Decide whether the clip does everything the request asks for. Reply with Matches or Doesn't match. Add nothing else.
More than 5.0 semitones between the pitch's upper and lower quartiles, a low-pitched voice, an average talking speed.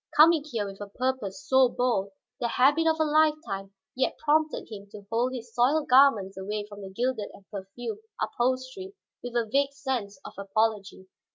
Doesn't match